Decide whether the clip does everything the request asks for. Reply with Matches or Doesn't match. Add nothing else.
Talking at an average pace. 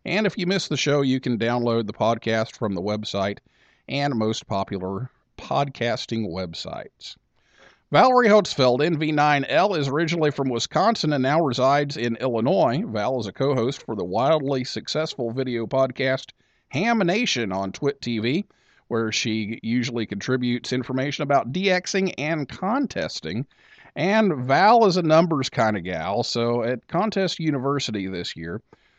Matches